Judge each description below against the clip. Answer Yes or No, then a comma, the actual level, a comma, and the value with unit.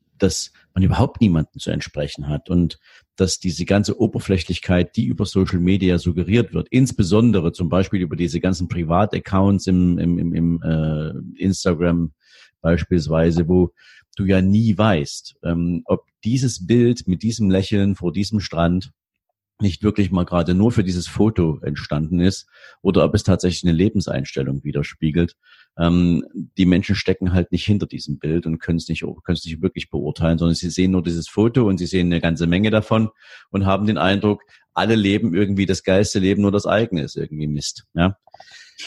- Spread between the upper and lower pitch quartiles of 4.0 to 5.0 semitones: No, average, 3.0 semitones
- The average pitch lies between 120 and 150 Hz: No, very low, 90 Hz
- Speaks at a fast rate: No, average, 175 wpm